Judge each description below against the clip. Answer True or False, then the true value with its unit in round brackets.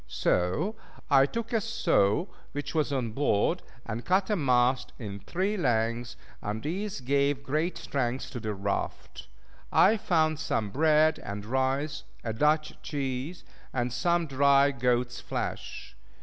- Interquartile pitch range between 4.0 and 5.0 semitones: True (4.7 semitones)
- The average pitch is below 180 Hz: True (140 Hz)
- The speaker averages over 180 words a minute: False (140 wpm)